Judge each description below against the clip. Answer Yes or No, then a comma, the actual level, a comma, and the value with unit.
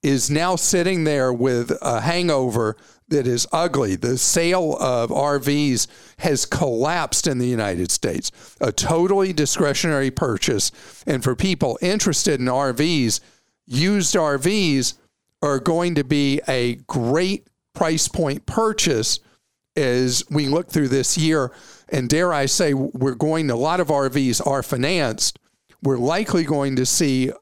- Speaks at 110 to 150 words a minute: Yes, average, 140 wpm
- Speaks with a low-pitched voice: No, medium, 145 Hz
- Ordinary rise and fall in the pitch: Yes, average, 4.6 semitones